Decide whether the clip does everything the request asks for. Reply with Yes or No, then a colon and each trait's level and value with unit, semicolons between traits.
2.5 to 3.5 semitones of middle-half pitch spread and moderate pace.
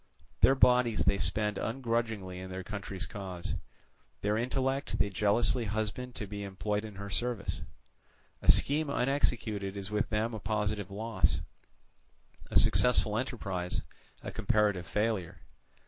No: average, 3.1 semitones; slow, 130 wpm